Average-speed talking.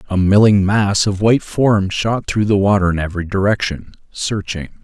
Yes: average, 175 wpm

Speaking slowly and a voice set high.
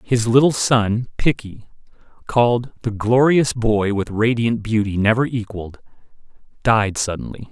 No: slow, 120 wpm; low, 115 Hz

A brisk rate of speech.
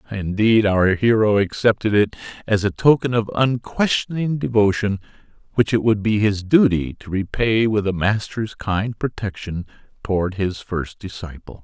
No: average, 145 wpm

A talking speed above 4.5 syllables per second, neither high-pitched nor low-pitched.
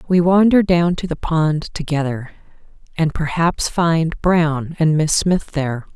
No: 4.0 syllables/s; medium, 160 Hz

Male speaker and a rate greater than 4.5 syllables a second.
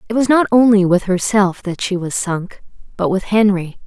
No: female; 4.9 syllables/s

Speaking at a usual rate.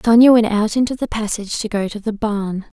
No: fast, 235 wpm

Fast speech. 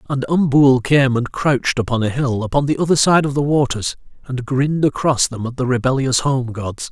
Yes: fast, 210 wpm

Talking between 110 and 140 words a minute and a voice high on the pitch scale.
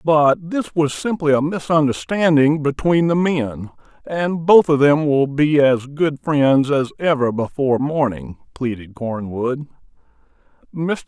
No: slow, 135 wpm; medium, 145 Hz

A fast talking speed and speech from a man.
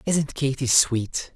No: slow, 135 wpm; male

